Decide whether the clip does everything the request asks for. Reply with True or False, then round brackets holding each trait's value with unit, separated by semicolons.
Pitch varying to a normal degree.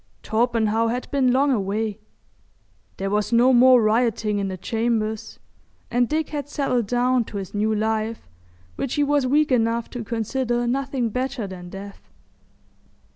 True (3.1 semitones)